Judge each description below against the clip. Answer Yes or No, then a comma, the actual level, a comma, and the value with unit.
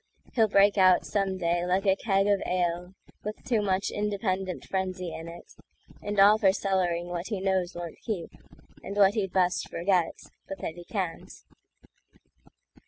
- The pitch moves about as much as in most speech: No, narrow, 2.2 semitones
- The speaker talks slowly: No, average, 145 wpm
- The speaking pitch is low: No, high, 190 Hz